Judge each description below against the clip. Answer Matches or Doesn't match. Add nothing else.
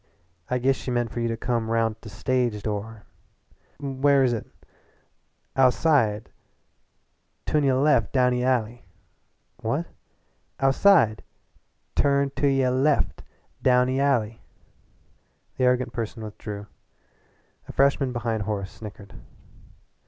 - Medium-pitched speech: Doesn't match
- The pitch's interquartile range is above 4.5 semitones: Doesn't match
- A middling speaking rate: Doesn't match